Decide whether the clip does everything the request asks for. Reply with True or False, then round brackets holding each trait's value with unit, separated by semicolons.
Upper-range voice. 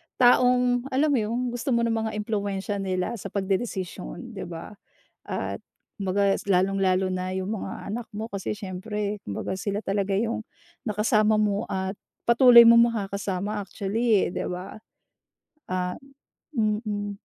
True (205 Hz)